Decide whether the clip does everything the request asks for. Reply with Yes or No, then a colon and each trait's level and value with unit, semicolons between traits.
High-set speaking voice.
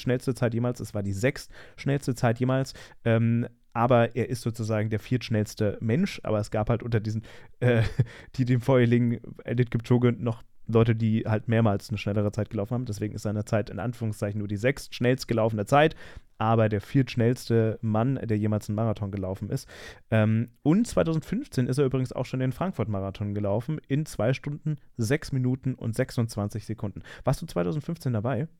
No: low, 115 Hz